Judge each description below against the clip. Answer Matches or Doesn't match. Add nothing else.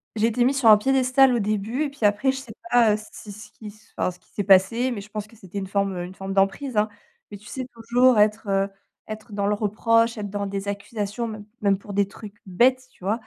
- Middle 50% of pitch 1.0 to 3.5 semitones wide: Matches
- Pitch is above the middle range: Matches